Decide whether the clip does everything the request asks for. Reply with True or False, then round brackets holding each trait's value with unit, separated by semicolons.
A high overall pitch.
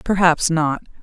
False (165 Hz)